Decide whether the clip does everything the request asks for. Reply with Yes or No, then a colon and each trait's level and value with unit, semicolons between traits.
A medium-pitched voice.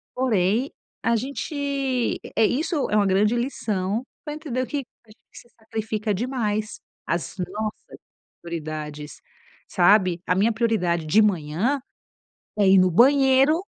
No: high, 220 Hz